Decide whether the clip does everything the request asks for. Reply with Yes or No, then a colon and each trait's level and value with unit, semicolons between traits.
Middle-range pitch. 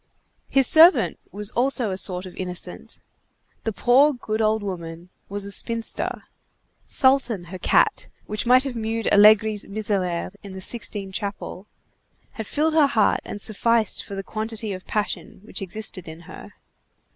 No: high, 210 Hz